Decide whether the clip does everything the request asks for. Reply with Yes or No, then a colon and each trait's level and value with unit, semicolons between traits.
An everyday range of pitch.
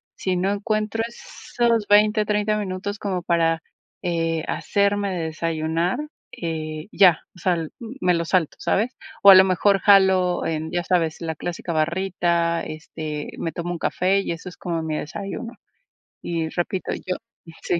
Yes: average, 3.4 semitones